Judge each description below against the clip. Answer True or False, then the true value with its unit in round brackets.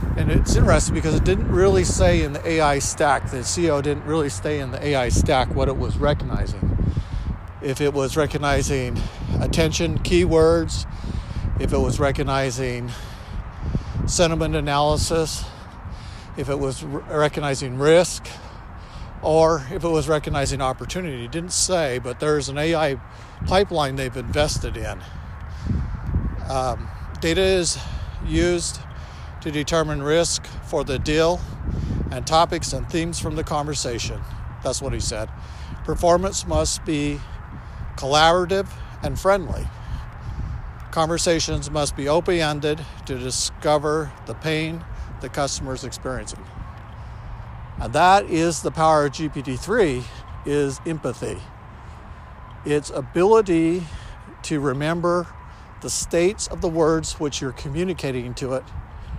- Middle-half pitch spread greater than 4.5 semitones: True (5.3 semitones)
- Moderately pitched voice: True (145 Hz)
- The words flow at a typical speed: False (125 wpm)